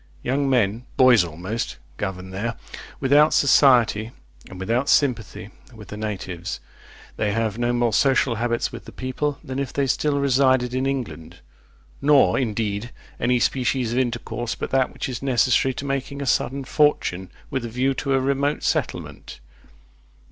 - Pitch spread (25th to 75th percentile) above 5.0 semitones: No, average, 3.5 semitones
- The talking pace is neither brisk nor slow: Yes, average, 155 wpm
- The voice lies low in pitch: Yes, low, 125 Hz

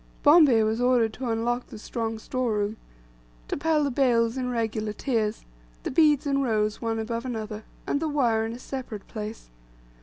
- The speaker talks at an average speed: Yes, average, 180 wpm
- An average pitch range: Yes, average, 3.0 semitones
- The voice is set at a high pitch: Yes, high, 230 Hz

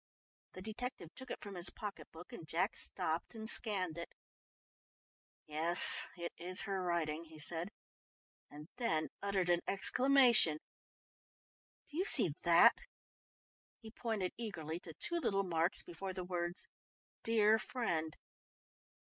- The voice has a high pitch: No, medium, 180 Hz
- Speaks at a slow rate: Yes, slow, 130 wpm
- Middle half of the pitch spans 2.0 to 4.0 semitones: No, average, 4.7 semitones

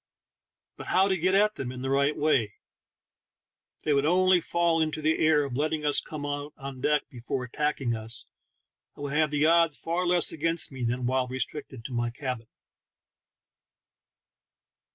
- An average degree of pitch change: Yes, average, 3.9 semitones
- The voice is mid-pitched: Yes, medium, 145 Hz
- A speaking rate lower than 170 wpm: No, average, 175 wpm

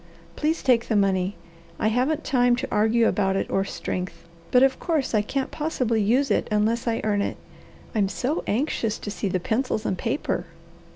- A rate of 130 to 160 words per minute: No, average, 185 wpm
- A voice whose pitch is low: No, high, 225 Hz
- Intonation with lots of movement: No, average, 3.9 semitones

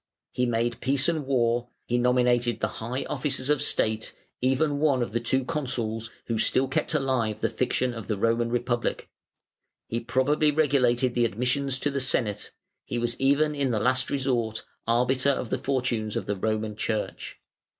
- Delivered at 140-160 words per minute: No, average, 170 wpm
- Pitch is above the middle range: No, low, 125 Hz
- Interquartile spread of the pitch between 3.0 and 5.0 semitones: No, narrow, 2.6 semitones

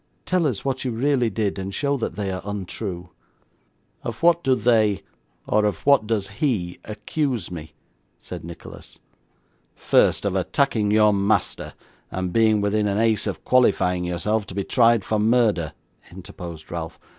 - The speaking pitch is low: Yes, low, 105 Hz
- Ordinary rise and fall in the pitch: Yes, average, 3.9 semitones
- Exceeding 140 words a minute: Yes, average, 155 wpm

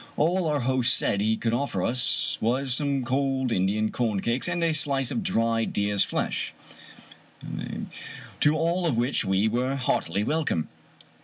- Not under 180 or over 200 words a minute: No, average, 155 wpm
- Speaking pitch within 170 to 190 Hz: No, low, 125 Hz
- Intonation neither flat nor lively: Yes, average, 4.6 semitones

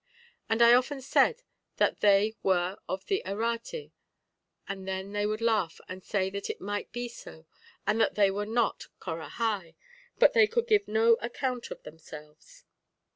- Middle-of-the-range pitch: No, high, 215 Hz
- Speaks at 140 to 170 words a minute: Yes, average, 165 wpm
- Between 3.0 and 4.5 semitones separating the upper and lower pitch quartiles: Yes, average, 4.1 semitones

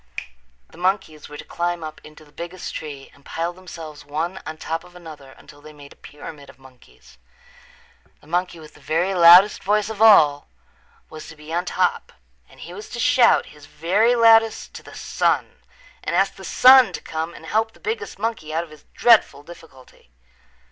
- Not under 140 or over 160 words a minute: No, average, 190 wpm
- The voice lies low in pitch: No, medium, 165 Hz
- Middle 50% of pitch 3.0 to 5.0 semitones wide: Yes, average, 4.6 semitones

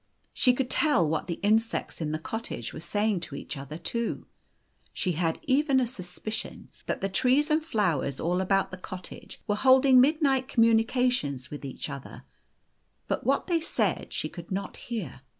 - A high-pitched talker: Yes, high, 210 Hz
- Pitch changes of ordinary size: No, wide, 7.3 semitones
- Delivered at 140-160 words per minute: No, average, 175 wpm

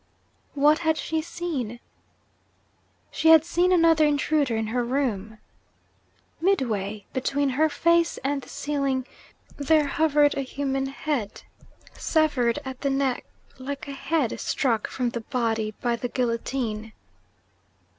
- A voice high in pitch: Yes, very high, 275 Hz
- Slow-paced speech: Yes, slow, 125 wpm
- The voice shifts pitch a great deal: No, average, 4.4 semitones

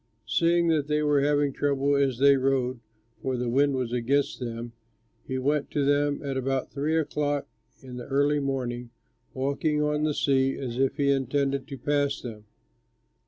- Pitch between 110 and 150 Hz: Yes, medium, 140 Hz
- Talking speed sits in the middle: Yes, average, 170 wpm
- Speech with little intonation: Yes, narrow, 1.8 semitones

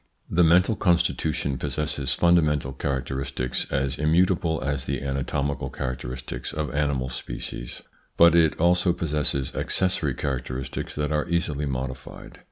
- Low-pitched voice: Yes, very low, 70 Hz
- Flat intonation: No, average, 3.8 semitones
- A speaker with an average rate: No, slow, 120 wpm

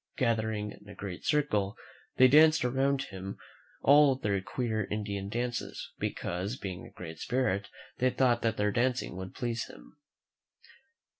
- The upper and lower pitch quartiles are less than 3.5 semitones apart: No, average, 4.4 semitones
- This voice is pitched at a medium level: No, low, 115 Hz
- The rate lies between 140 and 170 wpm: Yes, average, 145 wpm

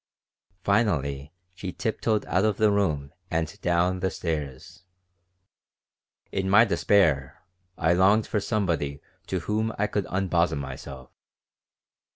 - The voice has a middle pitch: No, very low, 90 Hz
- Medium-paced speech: No, slow, 120 wpm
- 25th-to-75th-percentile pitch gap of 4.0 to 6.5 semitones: Yes, average, 5.2 semitones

